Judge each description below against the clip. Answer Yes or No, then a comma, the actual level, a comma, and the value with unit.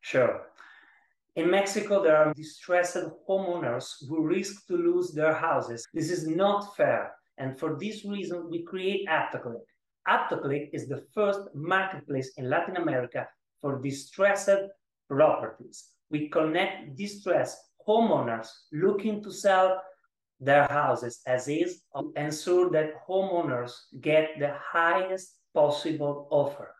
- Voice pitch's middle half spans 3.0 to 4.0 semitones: No, average, 4.7 semitones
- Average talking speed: No, slow, 125 wpm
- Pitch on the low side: No, medium, 170 Hz